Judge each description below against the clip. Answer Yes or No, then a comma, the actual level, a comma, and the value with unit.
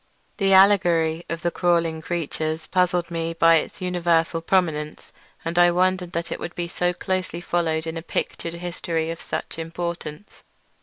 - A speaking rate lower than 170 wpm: Yes, average, 160 wpm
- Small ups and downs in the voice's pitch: Yes, narrow, 1.3 semitones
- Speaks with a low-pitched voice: No, medium, 170 Hz